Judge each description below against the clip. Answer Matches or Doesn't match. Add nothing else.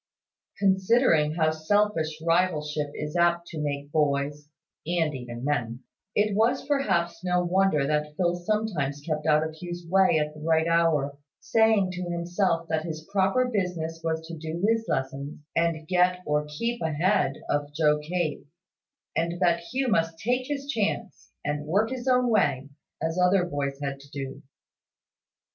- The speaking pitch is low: Doesn't match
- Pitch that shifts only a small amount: Doesn't match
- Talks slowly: Doesn't match